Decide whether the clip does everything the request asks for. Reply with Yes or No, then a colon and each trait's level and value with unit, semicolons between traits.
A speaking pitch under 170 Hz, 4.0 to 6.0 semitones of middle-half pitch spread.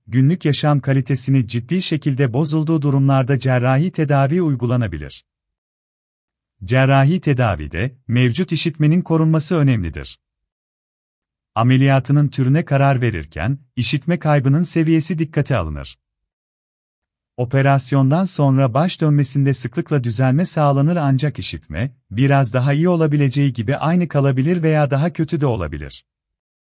Yes: low, 135 Hz; average, 5.3 semitones